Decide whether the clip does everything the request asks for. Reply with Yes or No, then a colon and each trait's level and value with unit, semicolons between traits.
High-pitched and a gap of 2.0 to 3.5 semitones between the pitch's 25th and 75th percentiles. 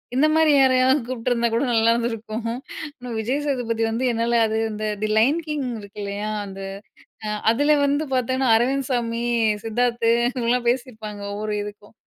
Yes: high, 240 Hz; average, 2.7 semitones